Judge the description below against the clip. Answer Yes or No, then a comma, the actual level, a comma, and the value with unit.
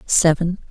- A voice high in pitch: No, medium, 170 Hz